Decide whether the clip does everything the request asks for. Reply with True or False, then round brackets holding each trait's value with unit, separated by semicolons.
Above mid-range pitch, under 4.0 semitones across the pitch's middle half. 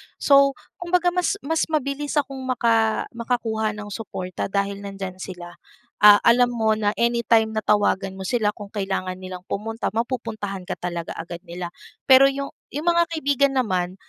False (220 Hz; 5.3 semitones)